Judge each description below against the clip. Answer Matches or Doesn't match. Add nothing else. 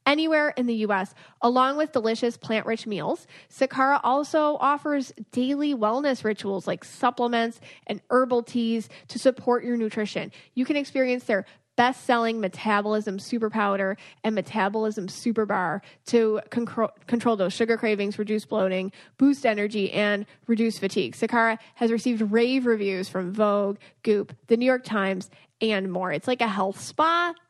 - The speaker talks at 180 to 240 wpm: Doesn't match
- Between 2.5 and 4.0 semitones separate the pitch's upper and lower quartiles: Matches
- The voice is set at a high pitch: Matches